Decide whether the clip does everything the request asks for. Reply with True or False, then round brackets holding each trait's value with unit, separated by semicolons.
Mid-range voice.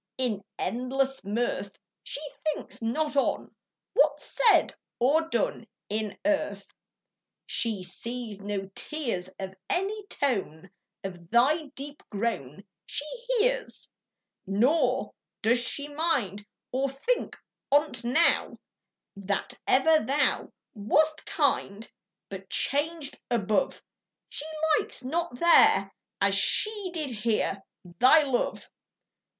False (255 Hz)